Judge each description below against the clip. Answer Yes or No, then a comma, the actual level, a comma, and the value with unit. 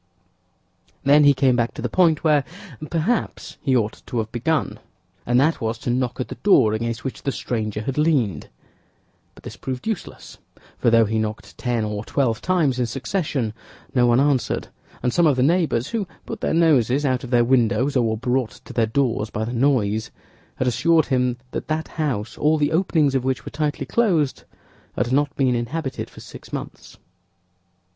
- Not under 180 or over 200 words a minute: Yes, average, 185 wpm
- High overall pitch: No, low, 130 Hz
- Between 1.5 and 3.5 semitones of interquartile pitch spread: No, average, 4.3 semitones